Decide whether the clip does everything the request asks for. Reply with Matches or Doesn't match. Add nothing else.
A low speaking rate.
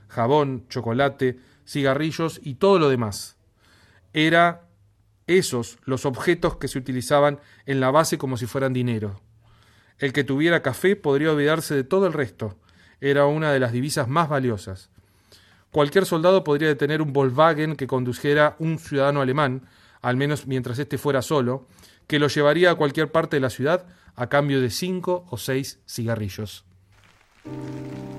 Doesn't match